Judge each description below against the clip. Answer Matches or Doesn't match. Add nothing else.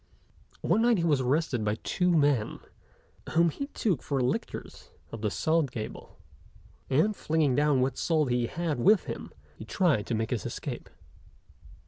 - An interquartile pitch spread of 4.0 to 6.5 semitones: Matches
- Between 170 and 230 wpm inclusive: Doesn't match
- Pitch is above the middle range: Doesn't match